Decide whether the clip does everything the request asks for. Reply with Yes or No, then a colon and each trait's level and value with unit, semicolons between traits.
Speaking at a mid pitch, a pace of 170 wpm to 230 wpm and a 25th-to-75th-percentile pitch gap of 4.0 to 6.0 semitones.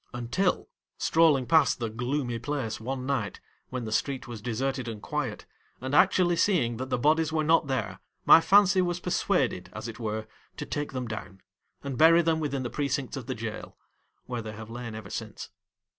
No: low, 130 Hz; average, 190 wpm; average, 5.0 semitones